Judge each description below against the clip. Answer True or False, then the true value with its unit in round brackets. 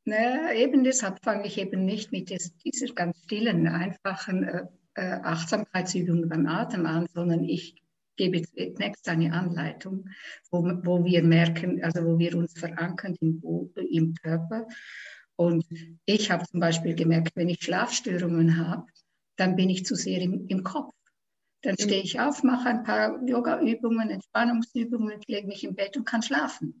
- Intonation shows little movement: False (4.9 semitones)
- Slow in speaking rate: False (155 wpm)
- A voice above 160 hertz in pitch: True (185 Hz)